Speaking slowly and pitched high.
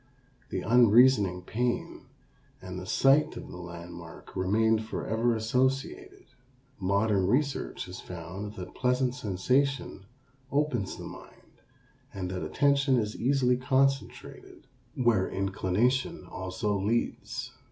No: slow, 110 wpm; low, 110 Hz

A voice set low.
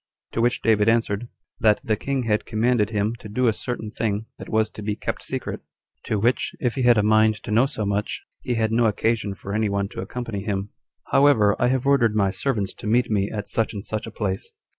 Yes: low, 110 Hz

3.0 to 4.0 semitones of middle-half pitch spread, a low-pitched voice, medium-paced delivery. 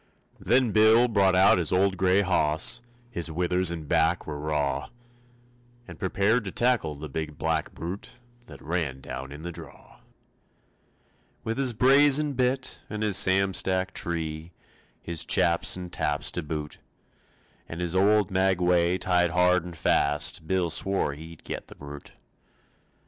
Yes: average, 3.6 semitones; very low, 90 Hz; average, 150 wpm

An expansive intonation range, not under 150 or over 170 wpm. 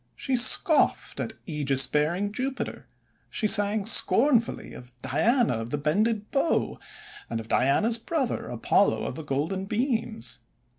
No: wide, 8.7 semitones; slow, 135 wpm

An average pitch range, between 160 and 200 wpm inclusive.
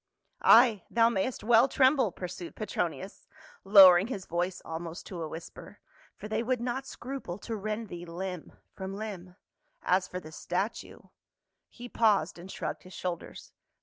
Yes: average, 4.7 semitones; average, 165 wpm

